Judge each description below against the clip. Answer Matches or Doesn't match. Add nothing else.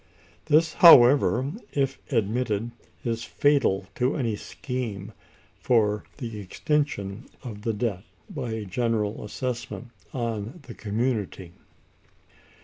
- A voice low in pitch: Matches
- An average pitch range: Matches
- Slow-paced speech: Matches